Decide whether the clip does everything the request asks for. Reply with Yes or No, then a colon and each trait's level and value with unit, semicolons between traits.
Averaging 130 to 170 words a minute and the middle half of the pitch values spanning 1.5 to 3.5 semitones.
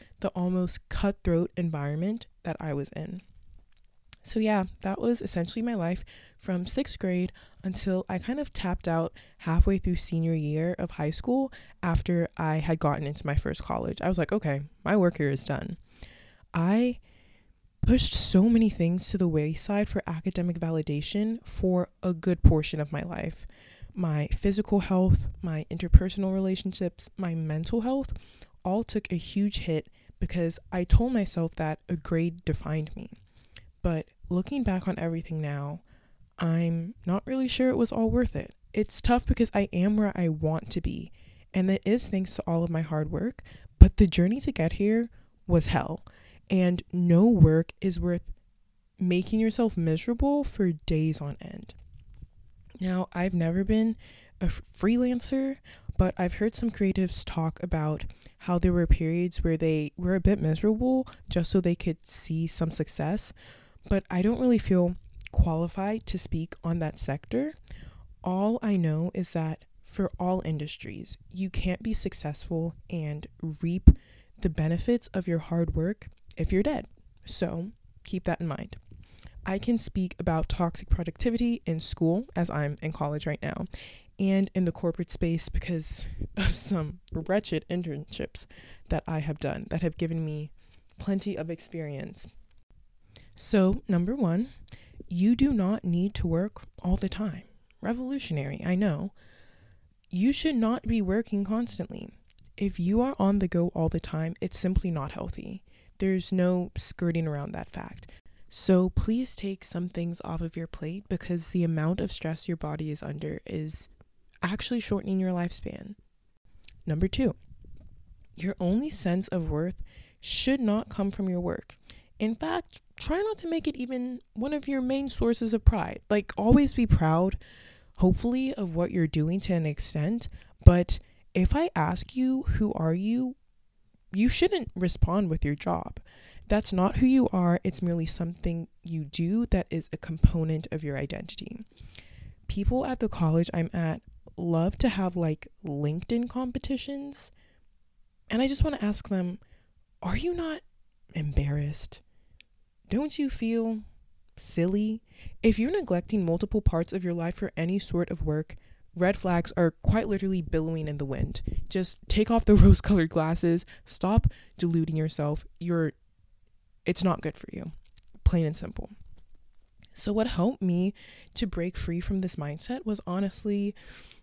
No: average, 160 wpm; average, 4.3 semitones